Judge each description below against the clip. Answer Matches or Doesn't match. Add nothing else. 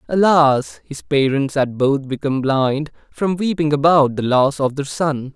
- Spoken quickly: Doesn't match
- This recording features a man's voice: Matches